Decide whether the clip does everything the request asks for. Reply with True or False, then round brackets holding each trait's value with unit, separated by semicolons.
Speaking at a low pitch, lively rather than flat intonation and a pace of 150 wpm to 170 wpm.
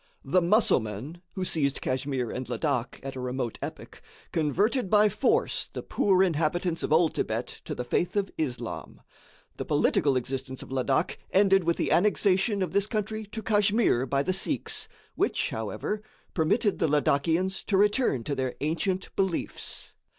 False (170 Hz; 6.9 semitones; 160 wpm)